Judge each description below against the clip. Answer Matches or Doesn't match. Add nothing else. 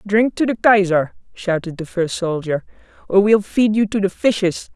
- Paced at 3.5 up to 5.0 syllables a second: Matches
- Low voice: Doesn't match